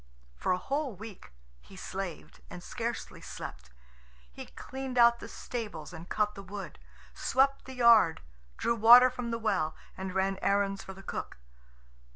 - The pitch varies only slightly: No, average, 4.2 semitones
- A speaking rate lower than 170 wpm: Yes, average, 160 wpm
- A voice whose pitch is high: Yes, high, 205 Hz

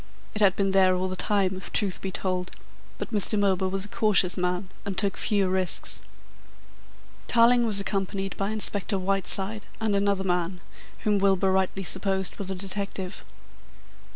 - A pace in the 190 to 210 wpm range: No, average, 165 wpm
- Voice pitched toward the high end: Yes, high, 195 Hz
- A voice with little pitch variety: Yes, narrow, 1.3 semitones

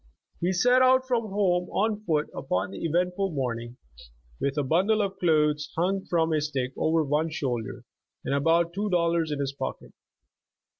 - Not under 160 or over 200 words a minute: Yes, average, 165 wpm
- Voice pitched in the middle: Yes, medium, 165 Hz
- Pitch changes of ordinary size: Yes, average, 4.7 semitones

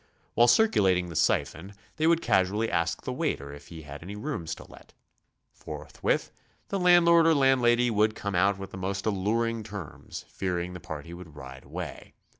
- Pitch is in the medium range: No, low, 100 Hz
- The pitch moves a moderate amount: No, wide, 5.8 semitones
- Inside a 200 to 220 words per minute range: No, average, 175 wpm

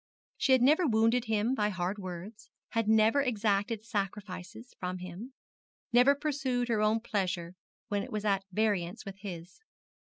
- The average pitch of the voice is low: No, high, 215 Hz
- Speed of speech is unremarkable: Yes, average, 155 wpm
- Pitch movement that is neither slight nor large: Yes, average, 3.7 semitones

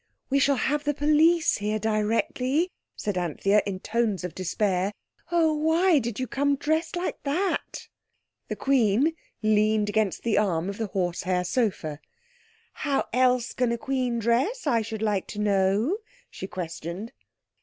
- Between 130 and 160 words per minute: Yes, average, 155 wpm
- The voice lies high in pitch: Yes, high, 230 Hz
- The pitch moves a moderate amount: No, wide, 6.1 semitones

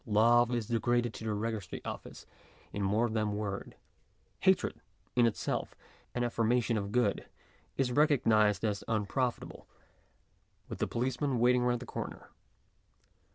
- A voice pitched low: Yes, low, 115 Hz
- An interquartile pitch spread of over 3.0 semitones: No, narrow, 2.4 semitones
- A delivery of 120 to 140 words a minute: Yes, slow, 135 wpm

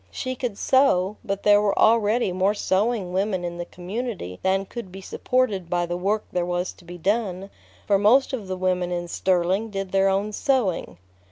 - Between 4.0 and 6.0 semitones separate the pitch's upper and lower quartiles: No, average, 3.1 semitones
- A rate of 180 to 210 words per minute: Yes, average, 190 wpm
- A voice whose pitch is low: No, high, 195 Hz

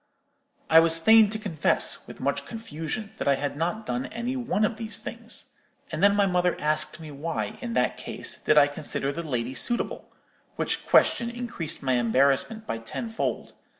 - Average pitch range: No, wide, 7.2 semitones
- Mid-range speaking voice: Yes, medium, 175 Hz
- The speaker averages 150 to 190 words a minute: Yes, average, 175 wpm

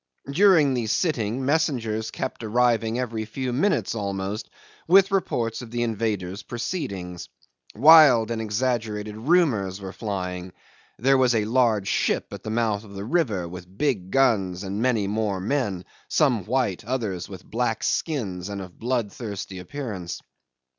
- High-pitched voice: No, low, 110 Hz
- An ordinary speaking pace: Yes, average, 145 wpm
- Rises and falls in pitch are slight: No, average, 4.5 semitones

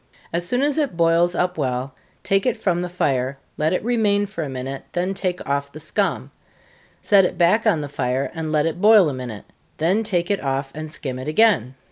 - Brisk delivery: Yes, fast, 215 wpm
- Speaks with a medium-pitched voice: Yes, medium, 165 Hz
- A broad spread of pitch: Yes, wide, 6.0 semitones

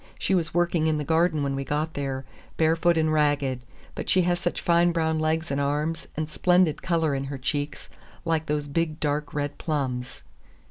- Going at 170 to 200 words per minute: Yes, average, 185 wpm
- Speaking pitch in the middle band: Yes, medium, 155 Hz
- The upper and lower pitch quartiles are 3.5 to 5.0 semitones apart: No, narrow, 2.5 semitones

